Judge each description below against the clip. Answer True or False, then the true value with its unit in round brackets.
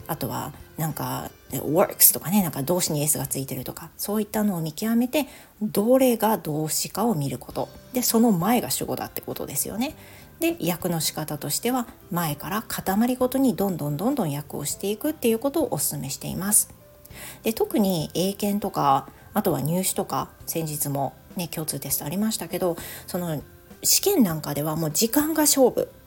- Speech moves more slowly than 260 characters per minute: False (365 characters per minute)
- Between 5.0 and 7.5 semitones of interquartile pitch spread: True (6.9 semitones)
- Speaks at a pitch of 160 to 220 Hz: True (190 Hz)